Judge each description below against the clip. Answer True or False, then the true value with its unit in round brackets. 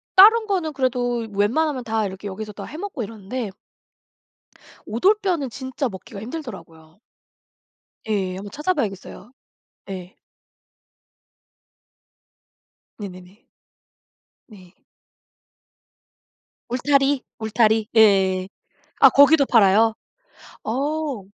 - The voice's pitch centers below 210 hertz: False (225 Hz)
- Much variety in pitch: True (6.0 semitones)